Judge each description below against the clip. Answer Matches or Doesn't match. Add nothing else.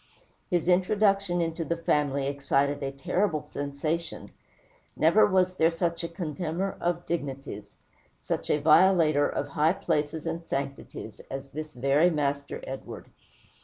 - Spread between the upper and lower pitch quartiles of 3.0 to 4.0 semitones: Matches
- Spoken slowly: Matches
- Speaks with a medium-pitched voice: Matches